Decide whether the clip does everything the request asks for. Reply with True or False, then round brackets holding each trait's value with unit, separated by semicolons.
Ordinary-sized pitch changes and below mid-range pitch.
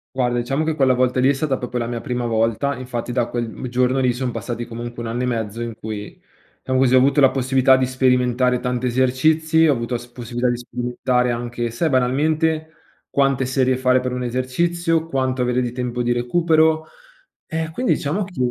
False (2.0 semitones; 125 Hz)